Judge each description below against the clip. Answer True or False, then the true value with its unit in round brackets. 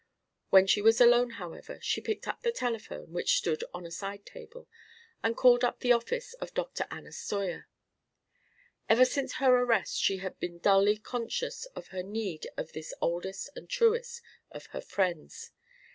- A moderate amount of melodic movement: False (7.1 semitones)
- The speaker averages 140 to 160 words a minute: False (170 wpm)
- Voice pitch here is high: True (230 Hz)